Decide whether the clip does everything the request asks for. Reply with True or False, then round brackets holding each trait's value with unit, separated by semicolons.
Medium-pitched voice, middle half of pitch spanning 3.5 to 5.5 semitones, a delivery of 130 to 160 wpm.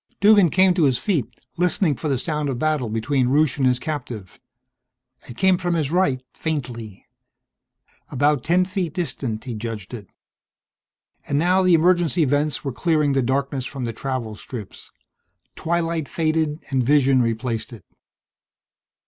True (145 Hz; 4.9 semitones; 150 wpm)